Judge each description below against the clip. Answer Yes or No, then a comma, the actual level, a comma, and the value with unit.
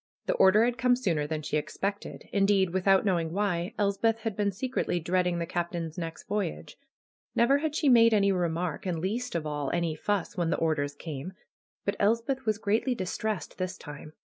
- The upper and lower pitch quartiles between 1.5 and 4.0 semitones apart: No, average, 4.5 semitones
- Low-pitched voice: No, high, 190 Hz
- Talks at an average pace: Yes, average, 190 wpm